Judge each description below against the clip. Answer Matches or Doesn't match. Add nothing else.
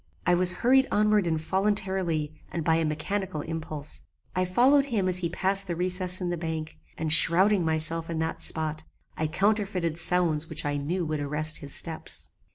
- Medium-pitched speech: Matches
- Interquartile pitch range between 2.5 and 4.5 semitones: Matches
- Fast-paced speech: Doesn't match